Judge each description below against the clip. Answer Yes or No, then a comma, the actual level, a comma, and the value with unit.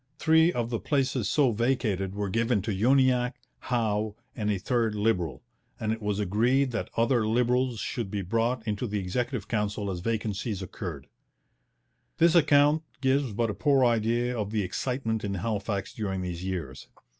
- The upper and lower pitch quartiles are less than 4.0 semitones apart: Yes, average, 3.5 semitones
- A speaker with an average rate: Yes, average, 165 wpm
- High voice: No, low, 115 Hz